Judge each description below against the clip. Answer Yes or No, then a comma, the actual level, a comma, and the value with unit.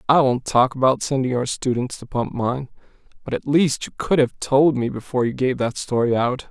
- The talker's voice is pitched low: Yes, low, 130 Hz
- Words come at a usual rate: No, fast, 220 wpm